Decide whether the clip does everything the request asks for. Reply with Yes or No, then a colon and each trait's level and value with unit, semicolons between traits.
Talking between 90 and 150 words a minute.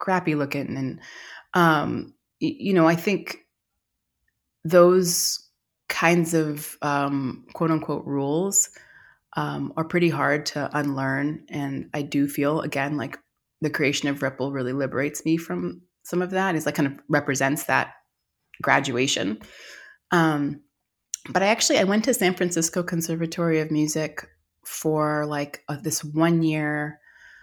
Yes: slow, 135 wpm